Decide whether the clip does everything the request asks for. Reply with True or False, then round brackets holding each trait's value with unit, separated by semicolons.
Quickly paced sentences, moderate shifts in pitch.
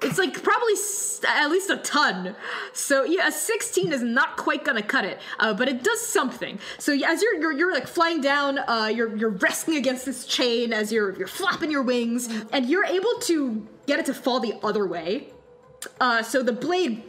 False (210 wpm; 7.3 semitones)